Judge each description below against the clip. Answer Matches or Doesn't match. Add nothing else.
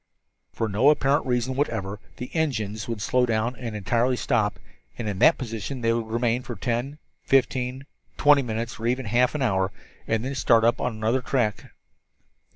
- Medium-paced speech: Matches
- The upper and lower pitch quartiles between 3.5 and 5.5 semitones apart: Doesn't match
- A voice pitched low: Matches